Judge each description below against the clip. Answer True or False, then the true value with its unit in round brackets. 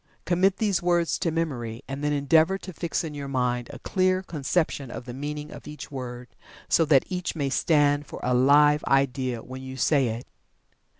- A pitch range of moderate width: True (4.1 semitones)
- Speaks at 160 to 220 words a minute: True (190 wpm)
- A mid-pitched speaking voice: True (145 Hz)